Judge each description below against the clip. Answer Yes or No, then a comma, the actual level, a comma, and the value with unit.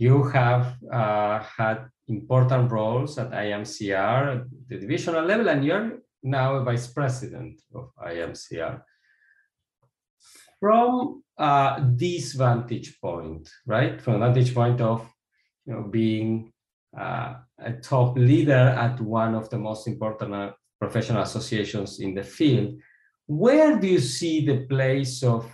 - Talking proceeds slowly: Yes, slow, 130 wpm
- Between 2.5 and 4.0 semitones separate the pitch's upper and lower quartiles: Yes, average, 3.4 semitones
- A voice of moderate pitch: No, low, 125 Hz